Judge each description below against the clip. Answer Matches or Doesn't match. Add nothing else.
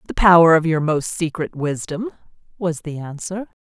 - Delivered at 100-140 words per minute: Doesn't match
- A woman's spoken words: Matches